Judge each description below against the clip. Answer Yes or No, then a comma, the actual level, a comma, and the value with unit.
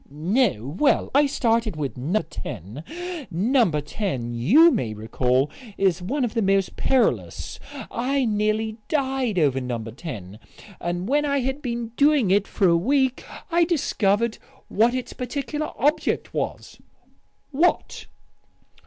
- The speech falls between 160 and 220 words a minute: No, slow, 135 wpm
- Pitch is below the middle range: No, high, 215 Hz